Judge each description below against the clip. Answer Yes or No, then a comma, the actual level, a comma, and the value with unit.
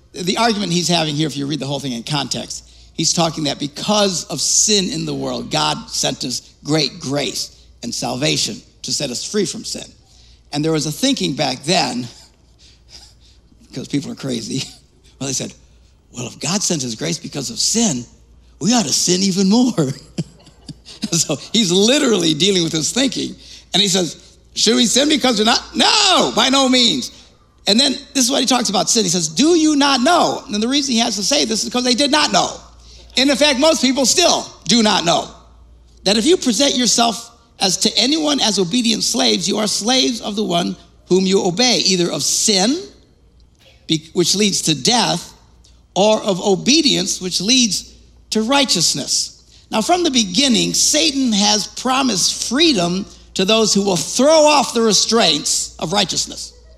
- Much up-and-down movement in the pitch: Yes, wide, 7.3 semitones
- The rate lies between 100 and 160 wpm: No, average, 185 wpm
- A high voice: Yes, high, 210 Hz